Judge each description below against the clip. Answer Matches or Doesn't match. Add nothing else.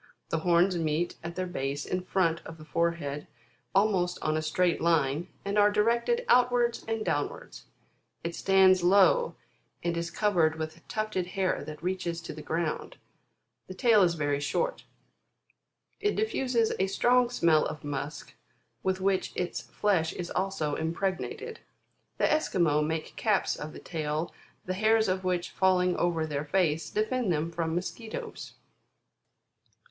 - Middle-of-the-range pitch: Matches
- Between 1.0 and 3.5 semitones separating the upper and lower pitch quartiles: Doesn't match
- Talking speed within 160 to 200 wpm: Doesn't match